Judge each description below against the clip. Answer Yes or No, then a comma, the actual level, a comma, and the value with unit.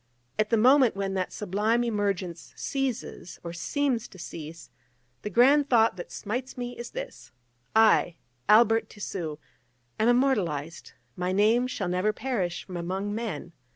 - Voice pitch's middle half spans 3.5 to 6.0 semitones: Yes, average, 5.0 semitones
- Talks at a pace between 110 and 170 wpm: Yes, average, 145 wpm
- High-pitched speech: Yes, high, 210 Hz